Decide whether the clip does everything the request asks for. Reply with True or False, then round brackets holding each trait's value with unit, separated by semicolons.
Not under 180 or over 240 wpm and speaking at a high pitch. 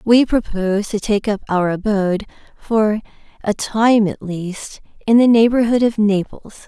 False (155 wpm; 210 Hz)